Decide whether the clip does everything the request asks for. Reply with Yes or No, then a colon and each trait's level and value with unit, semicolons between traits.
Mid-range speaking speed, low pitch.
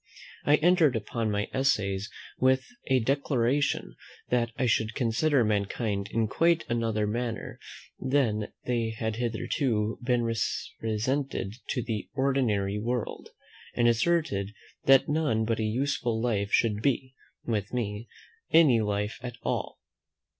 No: slow, 125 wpm; low, 115 Hz